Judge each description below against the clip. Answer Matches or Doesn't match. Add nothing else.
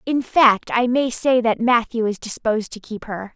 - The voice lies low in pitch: Doesn't match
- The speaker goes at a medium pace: Doesn't match